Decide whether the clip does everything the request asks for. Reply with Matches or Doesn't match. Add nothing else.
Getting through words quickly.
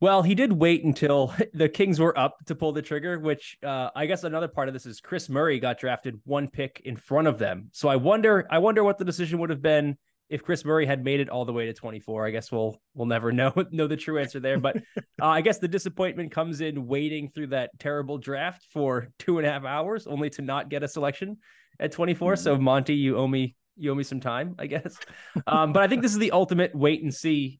Matches